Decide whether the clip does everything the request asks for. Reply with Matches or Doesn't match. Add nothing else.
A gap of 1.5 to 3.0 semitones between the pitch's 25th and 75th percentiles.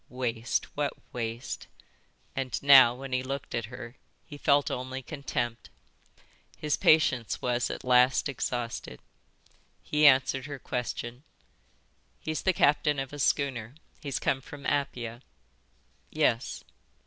Matches